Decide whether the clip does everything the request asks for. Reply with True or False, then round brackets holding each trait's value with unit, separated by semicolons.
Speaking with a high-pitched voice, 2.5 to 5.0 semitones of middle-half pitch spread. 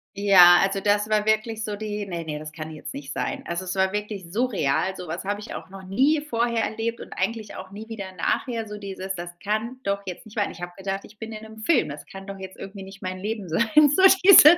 True (200 Hz; 2.8 semitones)